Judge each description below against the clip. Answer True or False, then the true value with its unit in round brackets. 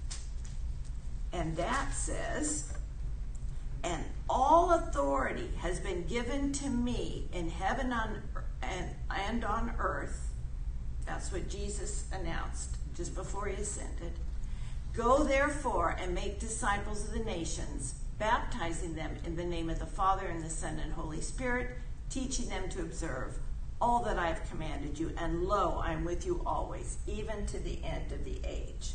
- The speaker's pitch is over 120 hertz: True (140 Hz)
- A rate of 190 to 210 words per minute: False (150 wpm)